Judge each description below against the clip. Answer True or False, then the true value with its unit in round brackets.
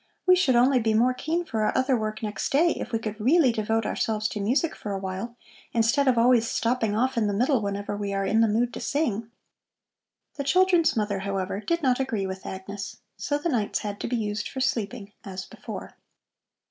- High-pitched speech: True (225 Hz)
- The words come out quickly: True (210 wpm)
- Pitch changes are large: False (4.1 semitones)